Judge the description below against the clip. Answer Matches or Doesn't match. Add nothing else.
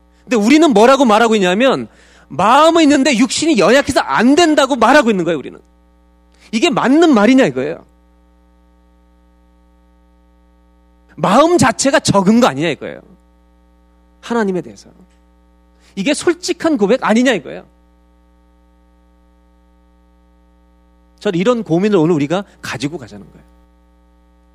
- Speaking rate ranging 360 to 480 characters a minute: Doesn't match